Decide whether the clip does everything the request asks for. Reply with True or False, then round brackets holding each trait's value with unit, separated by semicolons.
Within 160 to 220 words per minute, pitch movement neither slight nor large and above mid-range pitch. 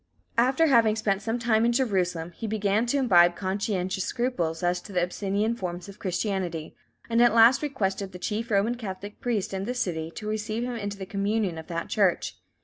True (195 wpm; 3.8 semitones; 205 Hz)